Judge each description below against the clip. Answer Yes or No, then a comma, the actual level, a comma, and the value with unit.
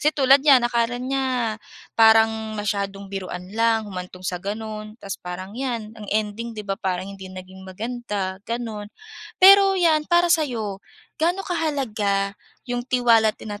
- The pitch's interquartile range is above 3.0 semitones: Yes, average, 4.0 semitones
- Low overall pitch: No, high, 220 Hz